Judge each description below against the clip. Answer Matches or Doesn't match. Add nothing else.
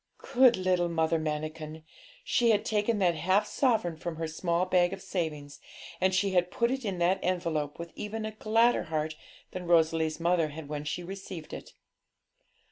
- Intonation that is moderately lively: Matches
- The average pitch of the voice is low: Doesn't match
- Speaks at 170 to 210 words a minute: Matches